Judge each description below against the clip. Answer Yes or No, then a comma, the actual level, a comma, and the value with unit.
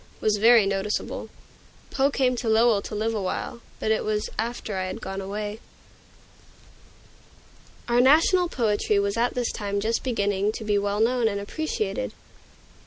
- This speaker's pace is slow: No, average, 155 wpm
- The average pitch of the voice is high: Yes, high, 215 Hz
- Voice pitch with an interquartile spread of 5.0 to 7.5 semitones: No, average, 2.9 semitones